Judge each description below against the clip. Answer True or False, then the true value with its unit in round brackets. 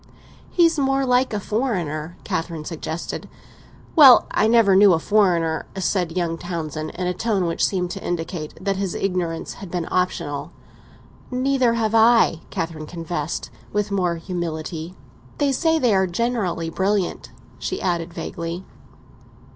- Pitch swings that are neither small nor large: True (4.9 semitones)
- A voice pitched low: False (180 Hz)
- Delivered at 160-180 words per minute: False (140 wpm)